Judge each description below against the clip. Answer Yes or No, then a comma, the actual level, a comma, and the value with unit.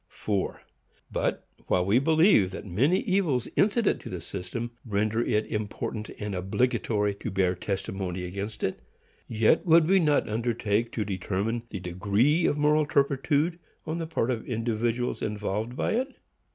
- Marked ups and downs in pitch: Yes, wide, 6.6 semitones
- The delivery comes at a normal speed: Yes, average, 150 wpm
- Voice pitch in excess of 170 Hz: No, low, 115 Hz